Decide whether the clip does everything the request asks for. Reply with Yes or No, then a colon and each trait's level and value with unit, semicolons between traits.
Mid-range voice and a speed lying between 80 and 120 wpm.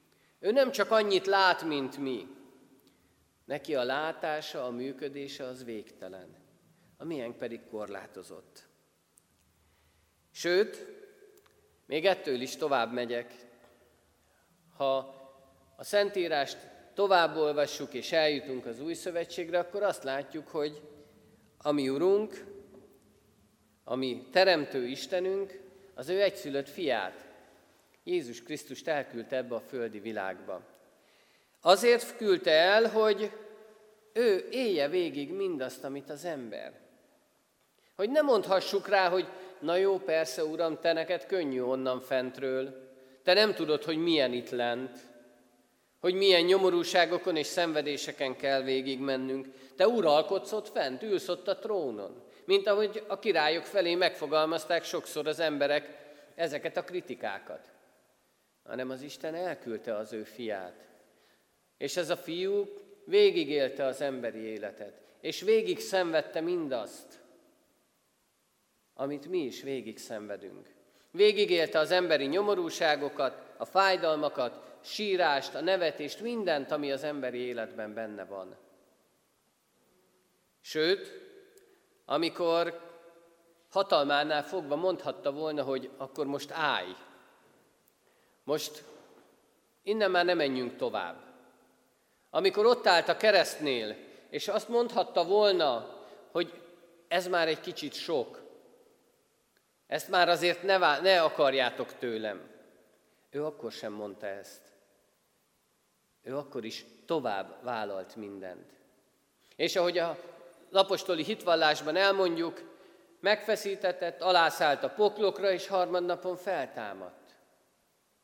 Yes: medium, 165 Hz; average, 110 wpm